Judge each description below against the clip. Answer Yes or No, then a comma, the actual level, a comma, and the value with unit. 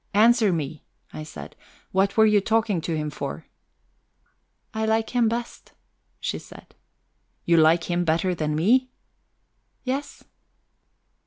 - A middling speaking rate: No, slow, 130 wpm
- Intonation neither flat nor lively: No, wide, 5.8 semitones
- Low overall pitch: No, high, 190 Hz